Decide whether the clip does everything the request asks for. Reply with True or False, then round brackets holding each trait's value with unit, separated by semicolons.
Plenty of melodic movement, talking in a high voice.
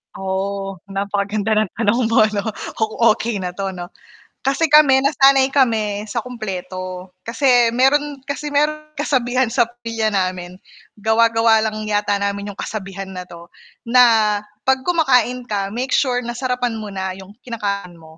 False (4.2 semitones; 220 Hz)